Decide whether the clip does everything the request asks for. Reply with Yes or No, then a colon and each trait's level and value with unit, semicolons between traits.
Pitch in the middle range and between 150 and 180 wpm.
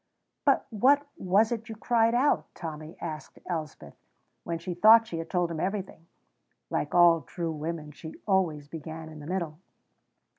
Yes: medium, 170 Hz; average, 160 wpm